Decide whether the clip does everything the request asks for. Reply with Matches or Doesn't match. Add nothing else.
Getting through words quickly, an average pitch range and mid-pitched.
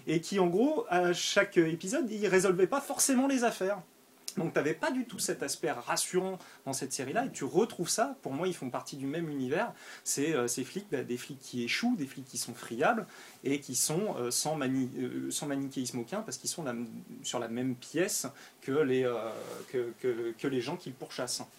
Doesn't match